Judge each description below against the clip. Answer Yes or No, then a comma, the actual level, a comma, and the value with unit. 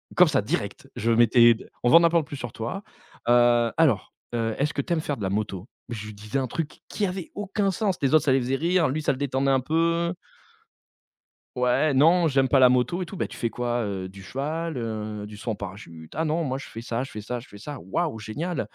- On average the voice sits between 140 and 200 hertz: No, low, 130 Hz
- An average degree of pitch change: No, wide, 6.0 semitones